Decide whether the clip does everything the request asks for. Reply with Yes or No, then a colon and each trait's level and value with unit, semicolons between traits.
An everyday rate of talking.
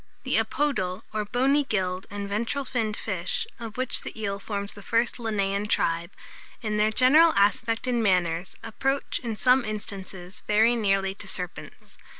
Yes: average, 155 wpm